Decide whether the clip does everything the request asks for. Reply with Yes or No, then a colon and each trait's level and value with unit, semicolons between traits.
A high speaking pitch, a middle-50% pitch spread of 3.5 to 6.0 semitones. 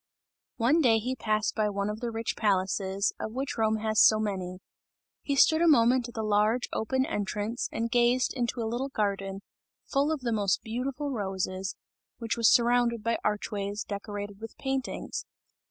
No: high, 220 Hz; average, 3.1 semitones